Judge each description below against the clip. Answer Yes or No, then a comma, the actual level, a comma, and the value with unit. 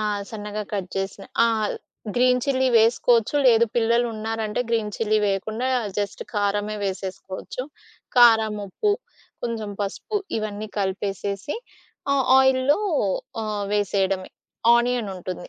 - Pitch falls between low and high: No, high, 215 Hz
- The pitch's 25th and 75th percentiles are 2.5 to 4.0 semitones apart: Yes, average, 3.1 semitones